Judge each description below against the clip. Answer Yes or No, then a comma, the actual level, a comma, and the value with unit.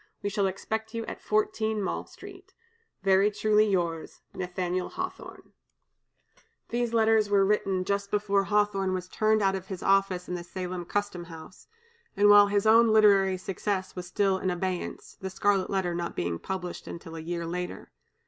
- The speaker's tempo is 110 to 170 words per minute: Yes, average, 165 wpm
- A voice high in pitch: Yes, high, 195 Hz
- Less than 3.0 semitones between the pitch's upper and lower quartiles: Yes, narrow, 2.4 semitones